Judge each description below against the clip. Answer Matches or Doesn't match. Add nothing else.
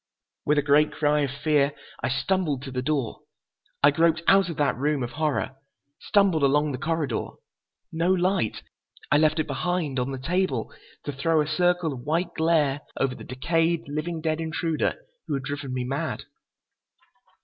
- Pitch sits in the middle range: Matches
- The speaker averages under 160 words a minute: Doesn't match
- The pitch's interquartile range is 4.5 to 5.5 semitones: Doesn't match